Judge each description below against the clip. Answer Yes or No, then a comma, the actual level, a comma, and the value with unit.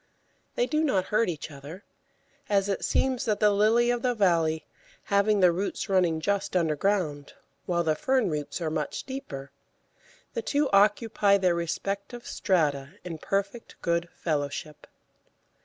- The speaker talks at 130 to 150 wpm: Yes, average, 145 wpm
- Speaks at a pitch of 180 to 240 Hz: Yes, high, 190 Hz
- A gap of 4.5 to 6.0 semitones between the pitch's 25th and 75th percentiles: Yes, average, 4.9 semitones